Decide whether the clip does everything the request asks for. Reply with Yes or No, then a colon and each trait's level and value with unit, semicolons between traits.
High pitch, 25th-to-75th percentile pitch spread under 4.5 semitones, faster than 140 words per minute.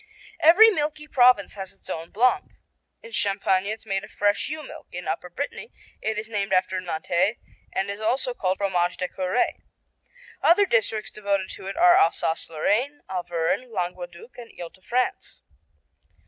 No: high, 205 Hz; wide, 5.5 semitones; average, 160 wpm